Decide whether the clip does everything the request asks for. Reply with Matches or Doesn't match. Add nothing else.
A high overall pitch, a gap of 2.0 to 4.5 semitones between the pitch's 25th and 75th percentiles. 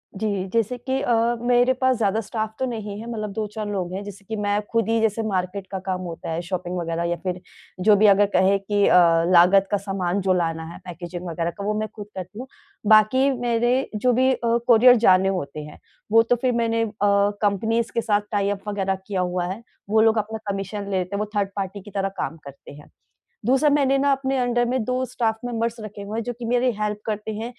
Matches